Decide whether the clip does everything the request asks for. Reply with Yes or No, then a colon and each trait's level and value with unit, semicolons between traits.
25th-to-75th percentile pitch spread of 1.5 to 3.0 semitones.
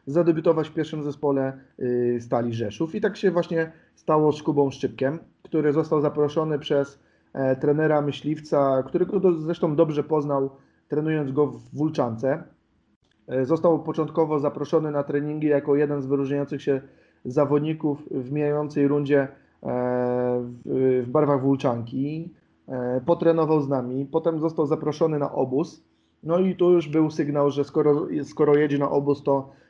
Yes: narrow, 2.4 semitones